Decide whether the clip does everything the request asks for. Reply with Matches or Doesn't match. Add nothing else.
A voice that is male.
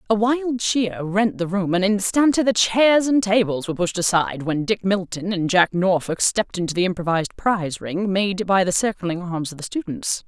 Doesn't match